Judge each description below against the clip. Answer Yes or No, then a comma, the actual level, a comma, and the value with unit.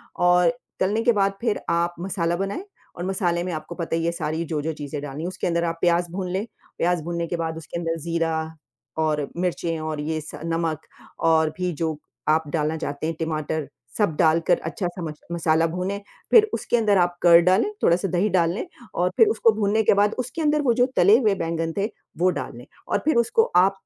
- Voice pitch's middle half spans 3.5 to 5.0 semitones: No, average, 3.1 semitones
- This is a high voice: No, medium, 170 Hz